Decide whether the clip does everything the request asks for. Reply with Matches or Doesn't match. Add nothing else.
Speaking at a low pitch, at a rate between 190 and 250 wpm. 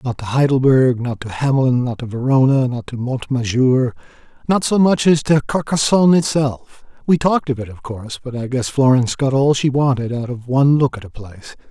Matches